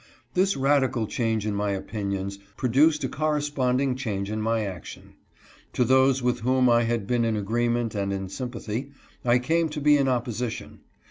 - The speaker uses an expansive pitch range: No, average, 3.6 semitones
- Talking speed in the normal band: Yes, average, 175 wpm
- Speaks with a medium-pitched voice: No, low, 120 Hz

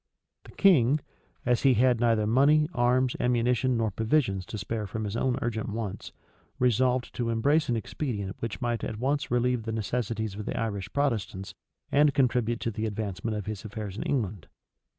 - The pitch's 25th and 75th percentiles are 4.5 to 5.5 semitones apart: No, average, 2.9 semitones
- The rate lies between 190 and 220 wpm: No, average, 175 wpm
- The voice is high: No, low, 115 Hz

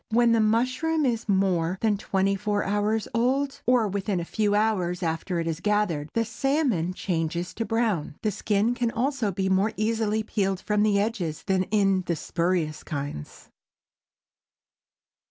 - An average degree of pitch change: Yes, average, 3.8 semitones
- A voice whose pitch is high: Yes, high, 205 Hz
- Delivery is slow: No, average, 155 wpm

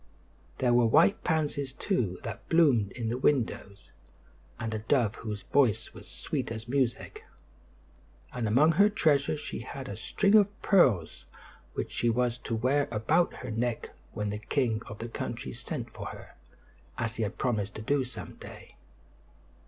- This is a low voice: Yes, low, 120 Hz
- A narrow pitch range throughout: No, average, 4.5 semitones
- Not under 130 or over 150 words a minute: No, average, 165 wpm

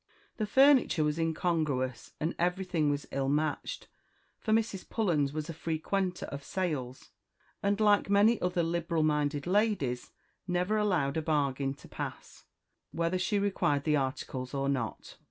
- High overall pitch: No, medium, 165 Hz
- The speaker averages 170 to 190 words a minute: No, average, 145 wpm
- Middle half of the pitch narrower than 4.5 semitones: No, average, 5.2 semitones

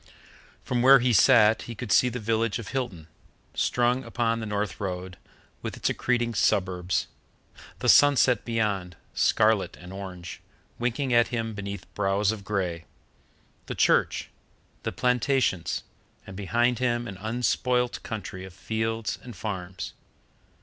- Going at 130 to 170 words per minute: Yes, slow, 135 wpm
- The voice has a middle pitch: No, low, 110 Hz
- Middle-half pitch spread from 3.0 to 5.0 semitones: Yes, average, 3.8 semitones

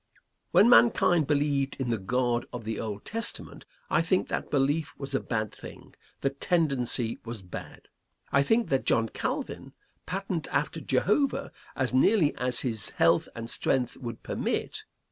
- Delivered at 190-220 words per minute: No, average, 155 wpm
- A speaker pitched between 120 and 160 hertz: Yes, low, 135 Hz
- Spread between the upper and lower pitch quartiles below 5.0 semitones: No, wide, 5.5 semitones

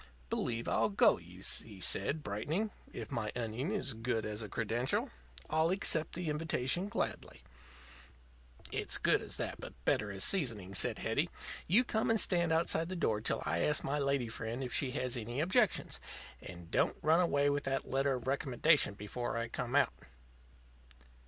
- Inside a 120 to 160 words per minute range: No, average, 170 wpm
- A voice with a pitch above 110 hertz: Yes, low, 135 Hz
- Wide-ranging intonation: Yes, wide, 6.1 semitones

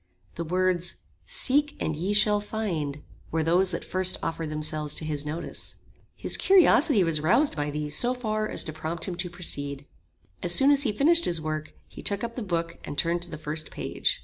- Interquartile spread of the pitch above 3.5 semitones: Yes, wide, 5.5 semitones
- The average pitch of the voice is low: No, medium, 175 Hz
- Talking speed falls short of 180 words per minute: No, average, 200 wpm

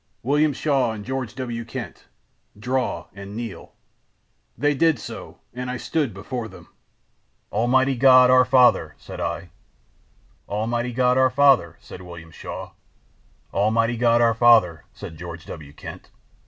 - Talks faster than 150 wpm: No, average, 140 wpm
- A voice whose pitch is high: No, low, 120 Hz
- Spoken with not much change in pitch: No, average, 3.9 semitones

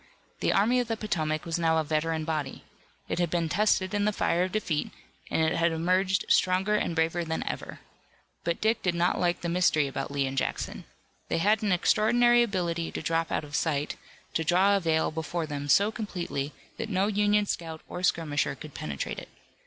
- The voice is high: No, medium, 170 Hz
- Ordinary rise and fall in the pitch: Yes, average, 3.9 semitones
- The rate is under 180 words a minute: No, average, 200 wpm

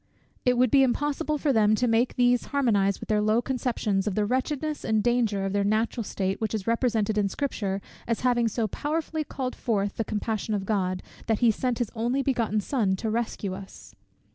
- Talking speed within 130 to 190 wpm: No, average, 200 wpm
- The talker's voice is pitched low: No, high, 225 Hz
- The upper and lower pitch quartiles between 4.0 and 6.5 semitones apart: No, average, 3.3 semitones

